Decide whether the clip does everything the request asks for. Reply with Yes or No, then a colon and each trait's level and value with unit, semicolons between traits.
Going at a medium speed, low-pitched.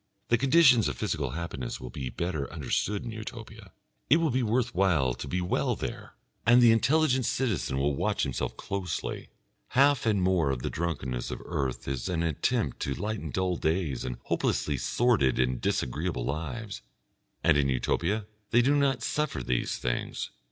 Yes: average, 170 wpm; very low, 90 Hz